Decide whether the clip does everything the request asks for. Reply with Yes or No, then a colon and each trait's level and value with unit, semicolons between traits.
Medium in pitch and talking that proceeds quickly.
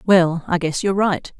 Yes: medium, 175 Hz; fast, 215 wpm